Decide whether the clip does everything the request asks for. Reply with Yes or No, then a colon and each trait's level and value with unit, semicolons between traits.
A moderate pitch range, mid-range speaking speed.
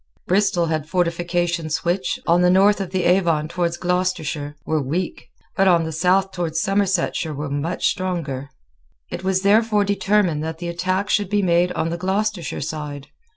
Yes: average, 3.0 semitones; average, 165 wpm